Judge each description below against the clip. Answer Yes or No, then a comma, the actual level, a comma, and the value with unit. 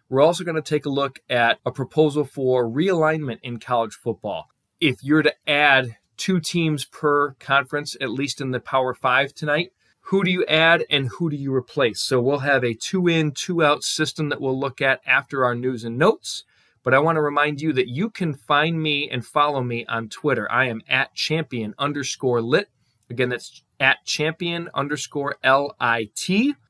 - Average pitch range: Yes, average, 3.4 semitones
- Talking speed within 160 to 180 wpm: No, average, 190 wpm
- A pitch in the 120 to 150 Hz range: Yes, medium, 140 Hz